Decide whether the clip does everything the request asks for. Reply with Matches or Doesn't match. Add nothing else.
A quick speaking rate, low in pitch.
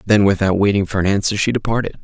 Matches